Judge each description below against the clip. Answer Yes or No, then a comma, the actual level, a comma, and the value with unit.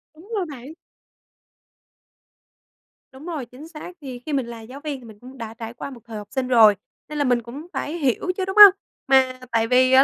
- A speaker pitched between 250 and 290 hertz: Yes, very high, 260 Hz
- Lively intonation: No, average, 4.1 semitones